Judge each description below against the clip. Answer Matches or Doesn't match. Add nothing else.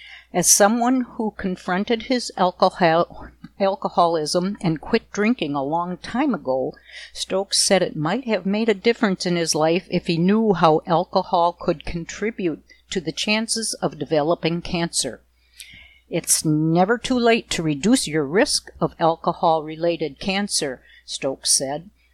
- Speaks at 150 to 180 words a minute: Doesn't match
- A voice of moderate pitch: Matches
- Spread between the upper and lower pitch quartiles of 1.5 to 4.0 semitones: Doesn't match